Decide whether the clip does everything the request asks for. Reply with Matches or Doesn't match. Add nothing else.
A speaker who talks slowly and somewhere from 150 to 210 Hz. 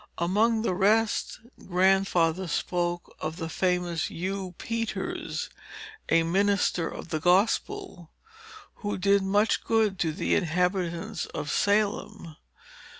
Matches